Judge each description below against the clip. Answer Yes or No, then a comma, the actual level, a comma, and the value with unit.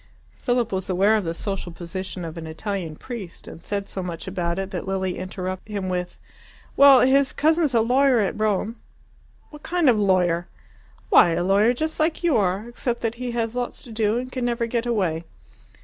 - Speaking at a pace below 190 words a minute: No, average, 195 wpm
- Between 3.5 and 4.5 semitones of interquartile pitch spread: No, average, 4.9 semitones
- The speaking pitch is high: Yes, high, 210 Hz